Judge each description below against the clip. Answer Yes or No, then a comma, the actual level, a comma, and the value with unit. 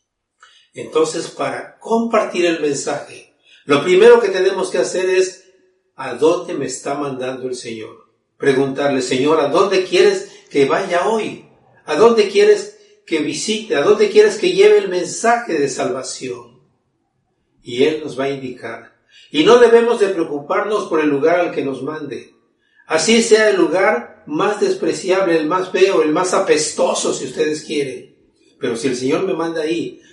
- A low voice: No, high, 195 Hz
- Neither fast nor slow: Yes, average, 160 wpm